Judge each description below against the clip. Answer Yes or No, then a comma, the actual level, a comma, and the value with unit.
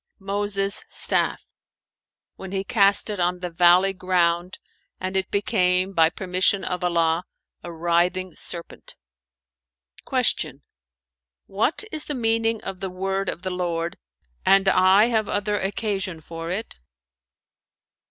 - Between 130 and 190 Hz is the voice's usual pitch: Yes, medium, 185 Hz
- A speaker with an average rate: No, slow, 125 wpm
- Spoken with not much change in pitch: Yes, narrow, 2.0 semitones